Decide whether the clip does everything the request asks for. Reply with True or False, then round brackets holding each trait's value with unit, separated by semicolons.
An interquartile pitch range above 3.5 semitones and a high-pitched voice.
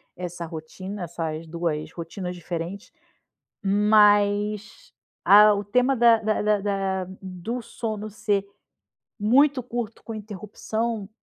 False (3.2 semitones; 205 Hz)